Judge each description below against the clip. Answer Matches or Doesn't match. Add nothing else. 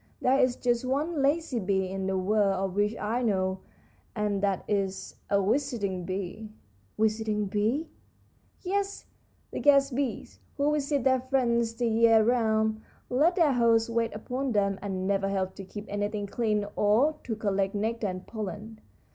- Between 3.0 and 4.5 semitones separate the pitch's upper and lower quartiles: Matches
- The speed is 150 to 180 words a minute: Matches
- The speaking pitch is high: Matches